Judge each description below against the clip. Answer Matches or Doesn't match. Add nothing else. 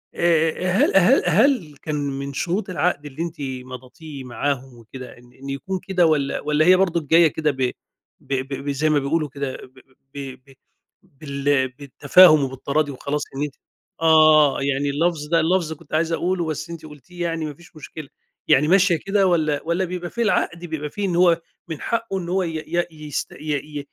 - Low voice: Doesn't match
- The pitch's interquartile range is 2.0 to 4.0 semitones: Matches